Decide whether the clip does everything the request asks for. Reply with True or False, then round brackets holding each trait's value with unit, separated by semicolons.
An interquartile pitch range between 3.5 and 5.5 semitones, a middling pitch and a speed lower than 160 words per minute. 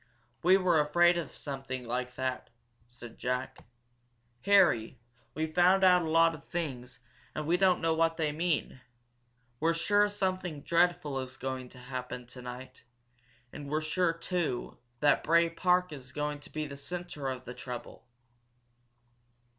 True (5.1 semitones; 155 Hz; 150 wpm)